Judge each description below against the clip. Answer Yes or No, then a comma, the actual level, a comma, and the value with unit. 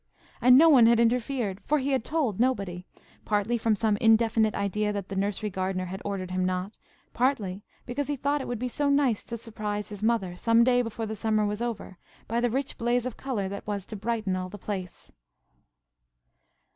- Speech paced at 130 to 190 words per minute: No, average, 200 wpm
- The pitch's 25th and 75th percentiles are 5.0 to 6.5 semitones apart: No, average, 3.5 semitones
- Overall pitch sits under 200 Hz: No, high, 220 Hz